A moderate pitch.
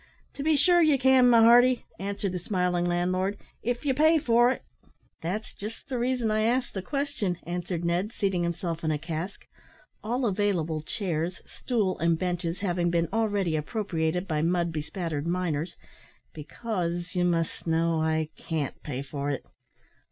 Yes: medium, 180 Hz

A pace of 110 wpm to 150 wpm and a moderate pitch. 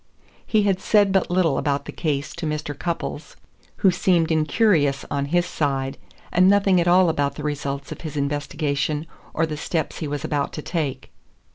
No: average, 180 wpm; medium, 155 Hz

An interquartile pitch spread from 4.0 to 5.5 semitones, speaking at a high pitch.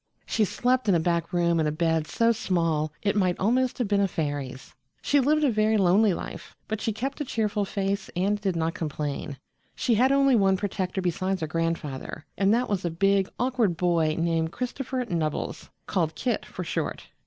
Yes: average, 5.1 semitones; high, 195 Hz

